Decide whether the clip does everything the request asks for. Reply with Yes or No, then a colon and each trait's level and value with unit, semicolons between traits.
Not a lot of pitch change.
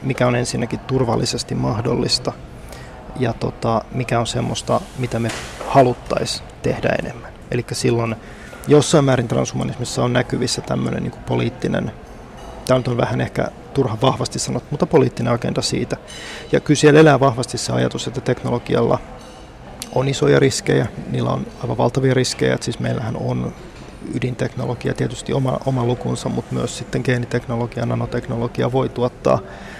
Yes: narrow, 1.9 semitones